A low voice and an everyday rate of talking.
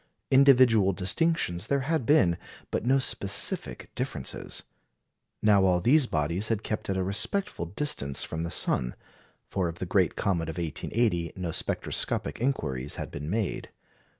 Yes: very low, 95 Hz; average, 150 wpm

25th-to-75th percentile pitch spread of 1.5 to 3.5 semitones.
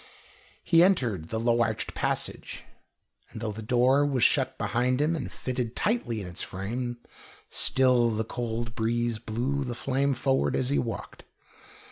Yes: average, 2.8 semitones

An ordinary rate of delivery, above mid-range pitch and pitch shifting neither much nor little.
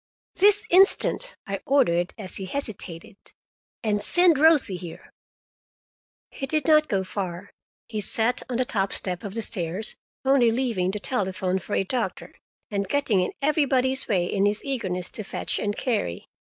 No: average, 160 wpm; high, 215 Hz; wide, 6.0 semitones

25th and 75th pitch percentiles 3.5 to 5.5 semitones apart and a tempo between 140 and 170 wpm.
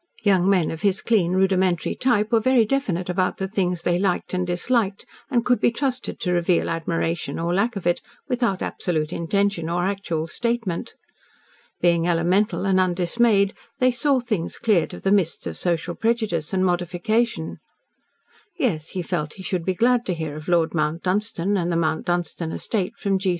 No: average, 3.8 semitones; average, 180 wpm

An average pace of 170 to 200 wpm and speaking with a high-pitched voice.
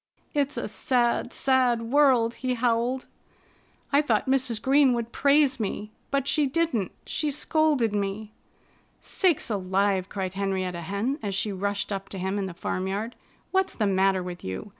No: average, 160 wpm; high, 230 Hz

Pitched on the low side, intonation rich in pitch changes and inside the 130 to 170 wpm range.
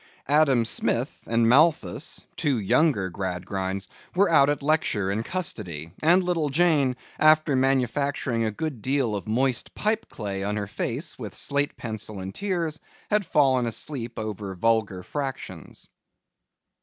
Yes: low, 125 Hz; wide, 6.5 semitones; average, 140 wpm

